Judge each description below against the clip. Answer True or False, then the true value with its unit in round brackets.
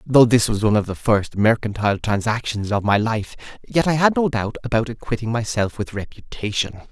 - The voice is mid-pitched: False (115 Hz)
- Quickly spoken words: False (190 wpm)